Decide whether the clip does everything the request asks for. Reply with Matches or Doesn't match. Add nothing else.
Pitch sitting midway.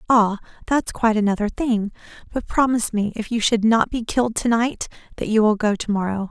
Doesn't match